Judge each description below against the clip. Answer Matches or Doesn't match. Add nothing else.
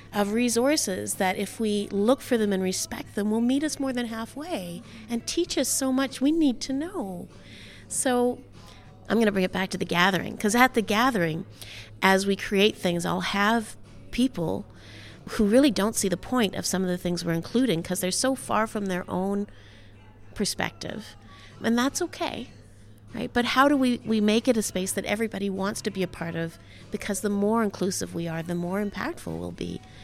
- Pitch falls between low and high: Doesn't match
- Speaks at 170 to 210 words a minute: Matches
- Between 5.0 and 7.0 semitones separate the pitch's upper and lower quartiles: Matches